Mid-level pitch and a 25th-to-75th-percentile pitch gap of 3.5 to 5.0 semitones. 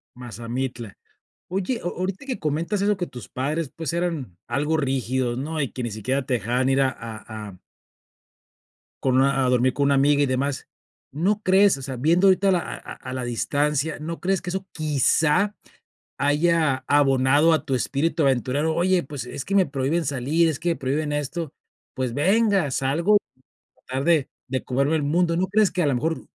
Yes: medium, 145 Hz; average, 4.6 semitones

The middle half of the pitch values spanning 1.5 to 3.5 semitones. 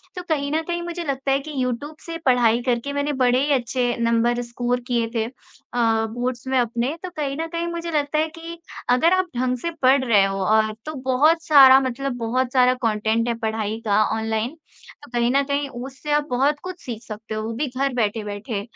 No: average, 3.9 semitones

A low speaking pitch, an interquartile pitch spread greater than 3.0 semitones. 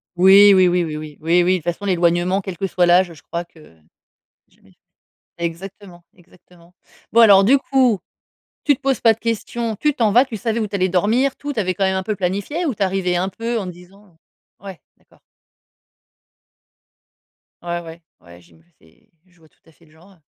No: medium, 185 Hz; average, 3.6 semitones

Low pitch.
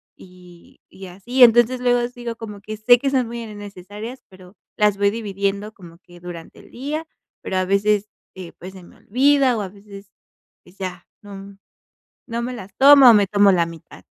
No: high, 205 Hz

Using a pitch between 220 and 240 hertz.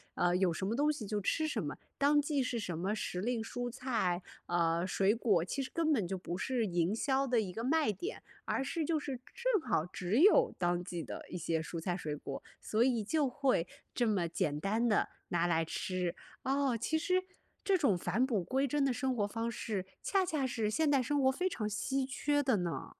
Yes: high, 230 Hz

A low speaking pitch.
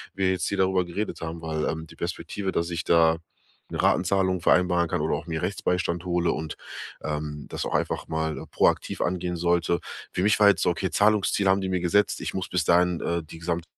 Yes: very low, 85 Hz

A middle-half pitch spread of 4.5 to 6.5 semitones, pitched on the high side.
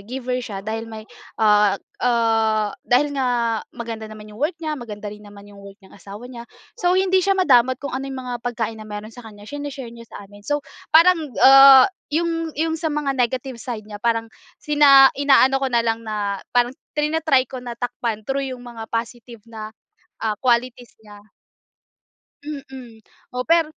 No: average, 3.9 semitones; high, 245 Hz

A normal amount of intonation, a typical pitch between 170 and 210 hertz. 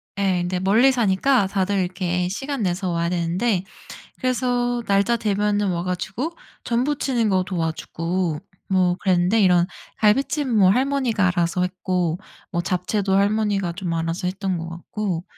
Yes: average, 3.6 semitones; high, 190 Hz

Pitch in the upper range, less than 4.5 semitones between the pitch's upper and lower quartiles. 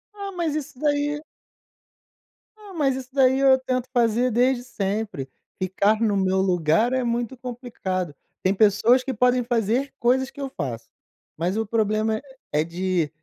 No: high, 235 Hz; average, 5.1 semitones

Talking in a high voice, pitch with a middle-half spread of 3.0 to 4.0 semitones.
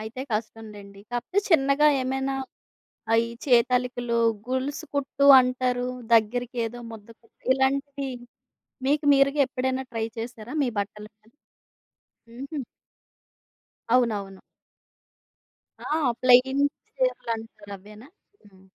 Yes: very high, 250 Hz; average, 3.3 semitones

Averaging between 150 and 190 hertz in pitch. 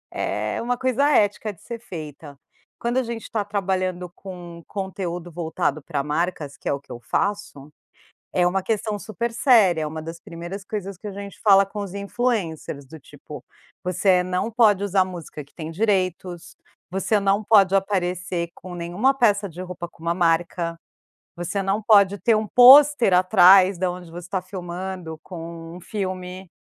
Yes: medium, 185 Hz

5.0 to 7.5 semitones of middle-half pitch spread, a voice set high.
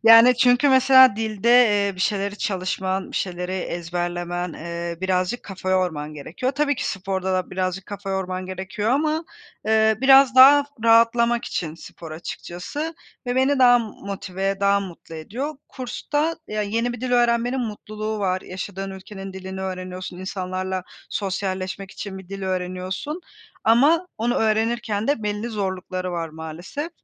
No: average, 4.4 semitones; high, 200 Hz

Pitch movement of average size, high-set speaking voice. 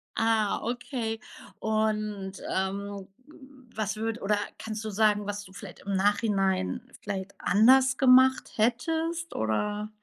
Yes: average, 3.1 semitones; high, 215 Hz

